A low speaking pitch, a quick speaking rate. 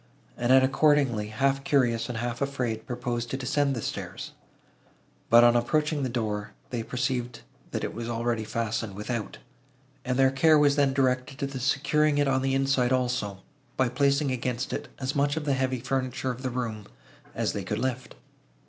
No: low, 130 Hz; average, 180 wpm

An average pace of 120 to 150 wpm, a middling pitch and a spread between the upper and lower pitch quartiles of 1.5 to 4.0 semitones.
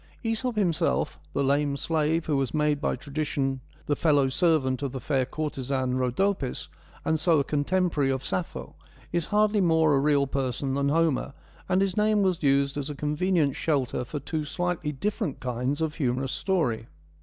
No: average, 170 wpm; medium, 150 Hz; average, 3.7 semitones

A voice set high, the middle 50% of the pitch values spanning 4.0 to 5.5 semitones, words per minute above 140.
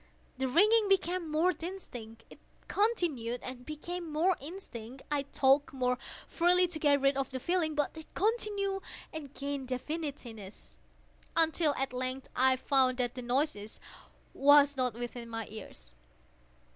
No: very high, 280 Hz; average, 5.1 semitones; slow, 135 wpm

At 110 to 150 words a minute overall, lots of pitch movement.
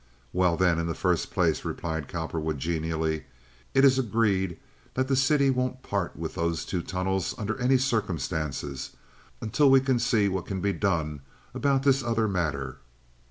No: average, 160 wpm; wide, 7.6 semitones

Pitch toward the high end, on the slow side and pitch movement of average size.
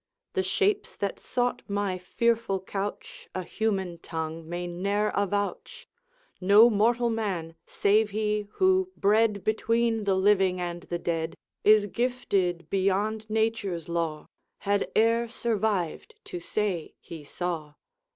Yes: high, 200 Hz; slow, 125 wpm; average, 3.8 semitones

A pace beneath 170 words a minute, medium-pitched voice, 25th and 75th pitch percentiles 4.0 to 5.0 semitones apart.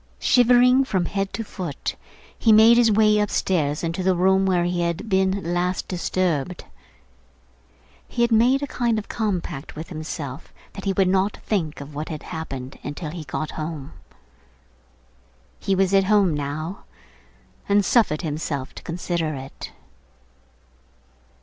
Yes: average, 145 wpm; medium, 180 Hz; average, 4.7 semitones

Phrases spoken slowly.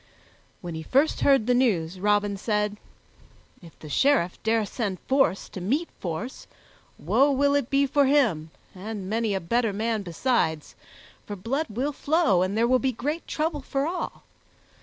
No: average, 165 wpm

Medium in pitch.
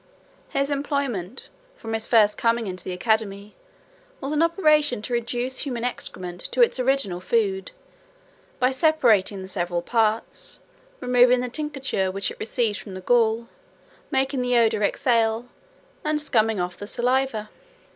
No: high, 235 Hz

